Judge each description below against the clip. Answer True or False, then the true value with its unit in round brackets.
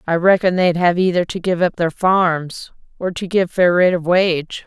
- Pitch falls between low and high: True (175 Hz)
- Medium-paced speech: False (220 wpm)